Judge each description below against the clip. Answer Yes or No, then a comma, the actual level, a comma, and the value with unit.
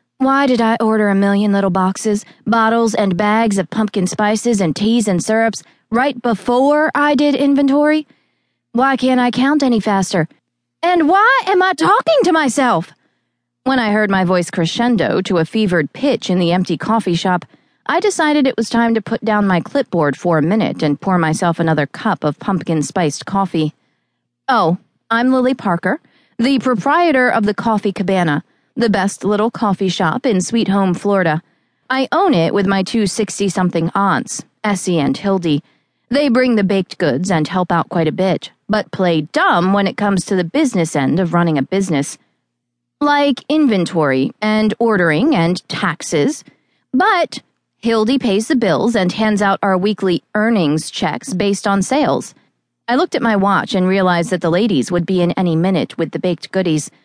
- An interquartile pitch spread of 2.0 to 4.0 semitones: No, average, 5.1 semitones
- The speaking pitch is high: Yes, high, 200 Hz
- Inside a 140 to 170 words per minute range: No, average, 180 wpm